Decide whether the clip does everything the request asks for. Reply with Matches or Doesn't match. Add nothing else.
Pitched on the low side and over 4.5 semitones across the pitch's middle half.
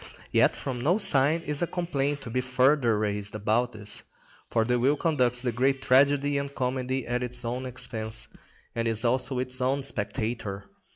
Doesn't match